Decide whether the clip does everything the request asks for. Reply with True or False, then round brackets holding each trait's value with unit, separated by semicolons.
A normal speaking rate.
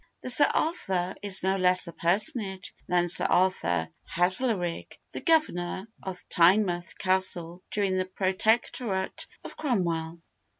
False (125 wpm)